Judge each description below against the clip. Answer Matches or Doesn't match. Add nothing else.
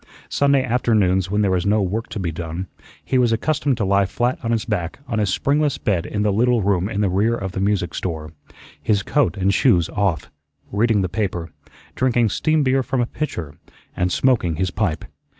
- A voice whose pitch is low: Matches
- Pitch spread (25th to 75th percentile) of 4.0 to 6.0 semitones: Matches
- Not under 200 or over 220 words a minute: Matches